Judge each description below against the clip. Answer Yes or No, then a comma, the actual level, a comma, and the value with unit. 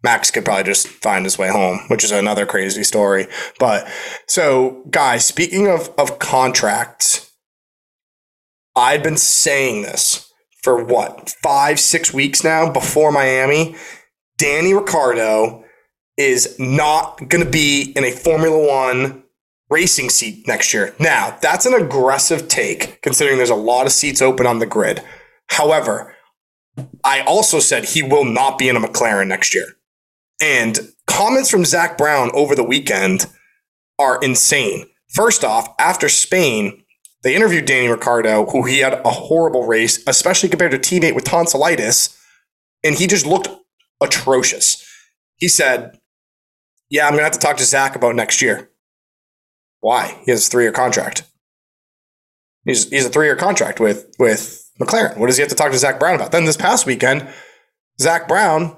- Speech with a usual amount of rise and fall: No, wide, 5.7 semitones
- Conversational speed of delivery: Yes, average, 160 wpm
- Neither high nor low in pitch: Yes, medium, 150 Hz